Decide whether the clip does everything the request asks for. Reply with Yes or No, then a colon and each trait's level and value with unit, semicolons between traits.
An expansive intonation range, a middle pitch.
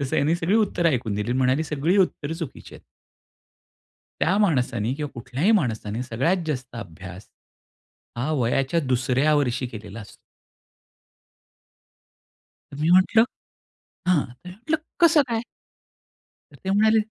Yes: wide, 6.7 semitones; medium, 145 Hz